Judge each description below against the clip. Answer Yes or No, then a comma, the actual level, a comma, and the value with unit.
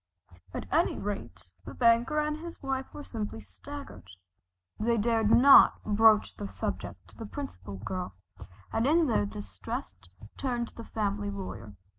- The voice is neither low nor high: No, high, 215 Hz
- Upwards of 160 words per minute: No, average, 150 wpm